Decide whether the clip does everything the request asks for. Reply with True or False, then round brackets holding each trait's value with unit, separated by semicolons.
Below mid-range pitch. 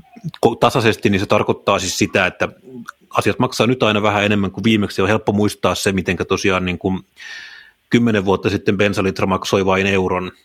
True (100 Hz)